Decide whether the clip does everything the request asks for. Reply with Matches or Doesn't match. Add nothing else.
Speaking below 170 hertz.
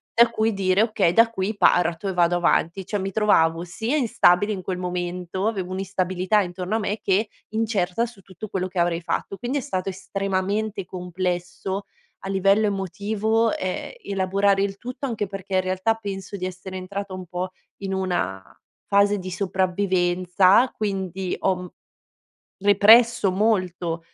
Doesn't match